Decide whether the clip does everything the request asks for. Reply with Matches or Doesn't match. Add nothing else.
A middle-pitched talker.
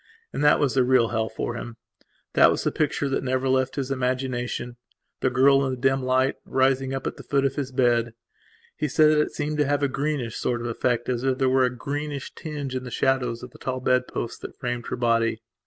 Doesn't match